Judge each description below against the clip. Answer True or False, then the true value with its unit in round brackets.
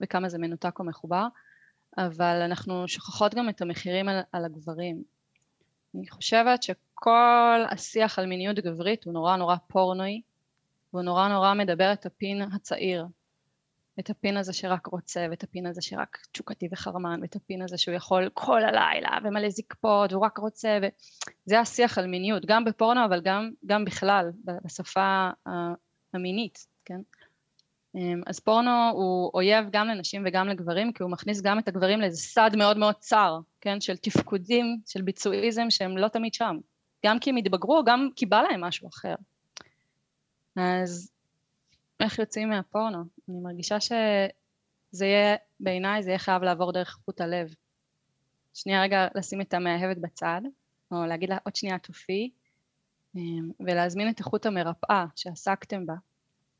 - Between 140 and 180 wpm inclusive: True (150 wpm)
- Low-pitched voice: False (190 Hz)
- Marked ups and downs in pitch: False (2.9 semitones)